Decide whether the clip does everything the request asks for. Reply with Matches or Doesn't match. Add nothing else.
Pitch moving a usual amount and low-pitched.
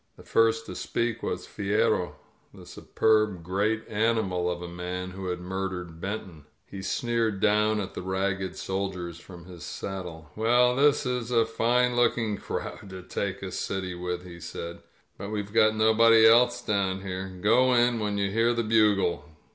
Matches